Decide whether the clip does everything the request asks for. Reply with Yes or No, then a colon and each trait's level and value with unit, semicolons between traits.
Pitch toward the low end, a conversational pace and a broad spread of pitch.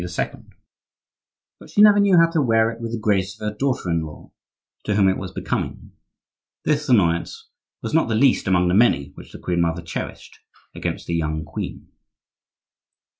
Yes: low, 105 Hz; average, 175 wpm; wide, 6.9 semitones